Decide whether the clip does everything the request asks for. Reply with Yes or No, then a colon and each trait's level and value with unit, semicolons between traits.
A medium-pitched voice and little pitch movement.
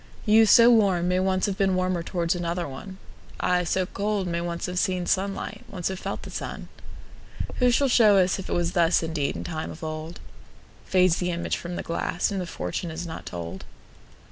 Yes: medium, 180 Hz; narrow, 2.1 semitones